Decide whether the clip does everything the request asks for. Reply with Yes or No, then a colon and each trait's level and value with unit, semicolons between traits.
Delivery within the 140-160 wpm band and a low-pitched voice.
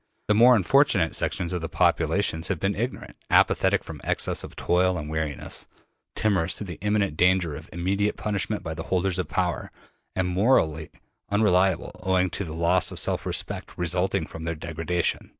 No: average, 170 wpm; very low, 90 Hz